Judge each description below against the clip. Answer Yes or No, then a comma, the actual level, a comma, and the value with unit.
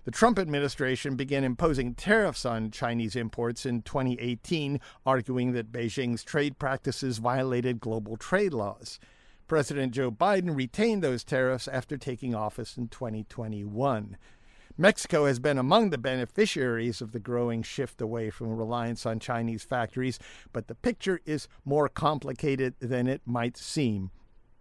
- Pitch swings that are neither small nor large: Yes, average, 3.2 semitones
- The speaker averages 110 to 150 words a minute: Yes, average, 140 wpm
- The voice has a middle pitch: No, low, 130 Hz